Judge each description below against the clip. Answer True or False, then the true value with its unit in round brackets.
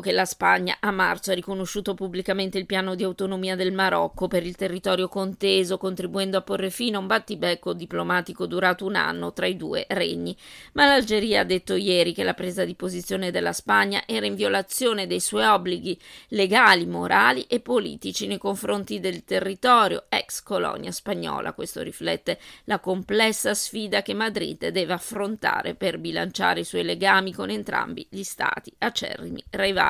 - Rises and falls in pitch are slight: True (1.8 semitones)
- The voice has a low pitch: False (190 Hz)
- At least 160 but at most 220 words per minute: True (165 wpm)